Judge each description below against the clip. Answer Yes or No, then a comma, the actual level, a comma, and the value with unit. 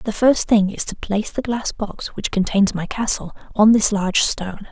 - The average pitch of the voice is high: Yes, high, 210 Hz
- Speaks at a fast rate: Yes, fast, 215 wpm